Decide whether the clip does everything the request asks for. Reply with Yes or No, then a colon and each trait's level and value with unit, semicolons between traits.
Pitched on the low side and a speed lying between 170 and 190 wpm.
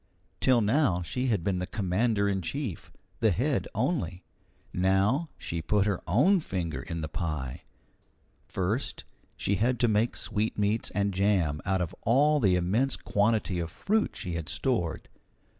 No: low, 100 Hz; average, 155 wpm